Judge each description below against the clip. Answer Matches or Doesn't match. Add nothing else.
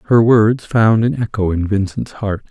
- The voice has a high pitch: Doesn't match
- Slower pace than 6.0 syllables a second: Matches